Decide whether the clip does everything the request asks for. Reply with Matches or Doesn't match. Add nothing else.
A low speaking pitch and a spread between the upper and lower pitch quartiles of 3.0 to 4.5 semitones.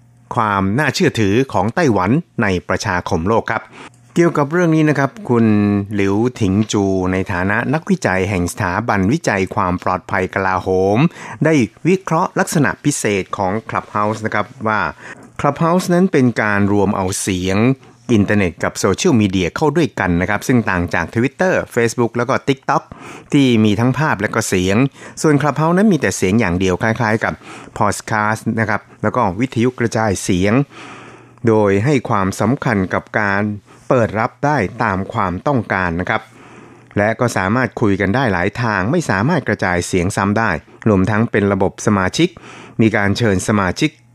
Doesn't match